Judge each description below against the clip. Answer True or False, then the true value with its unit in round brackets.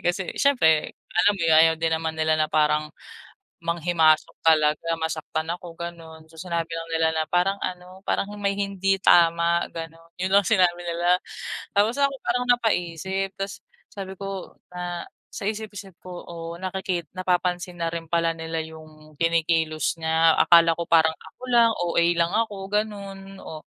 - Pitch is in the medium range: True (170 Hz)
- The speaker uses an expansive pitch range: False (2.8 semitones)